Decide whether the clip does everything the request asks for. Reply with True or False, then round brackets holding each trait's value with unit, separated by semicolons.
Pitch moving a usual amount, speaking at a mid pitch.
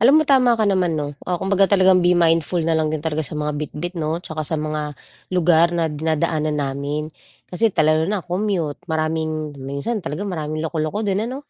True (3.5 semitones; 160 Hz)